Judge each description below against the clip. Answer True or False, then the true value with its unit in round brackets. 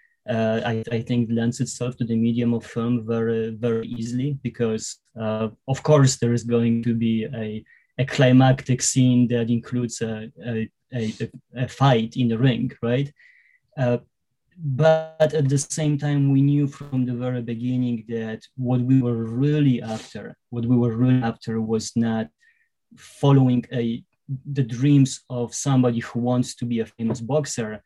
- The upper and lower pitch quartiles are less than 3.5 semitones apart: True (2.6 semitones)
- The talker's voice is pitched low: True (120 Hz)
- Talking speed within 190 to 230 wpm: False (165 wpm)